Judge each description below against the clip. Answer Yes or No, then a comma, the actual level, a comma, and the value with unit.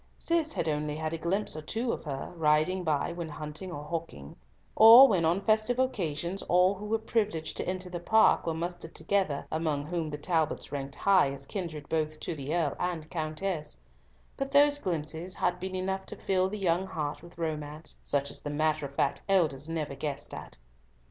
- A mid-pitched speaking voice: Yes, medium, 165 Hz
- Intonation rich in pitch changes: No, average, 3.9 semitones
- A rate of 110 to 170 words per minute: No, average, 195 wpm